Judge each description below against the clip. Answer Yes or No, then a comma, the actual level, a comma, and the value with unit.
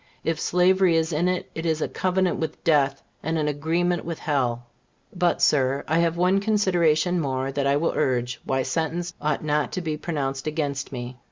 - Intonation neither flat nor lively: Yes, average, 3.8 semitones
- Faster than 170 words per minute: Yes, average, 190 wpm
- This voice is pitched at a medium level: Yes, medium, 160 Hz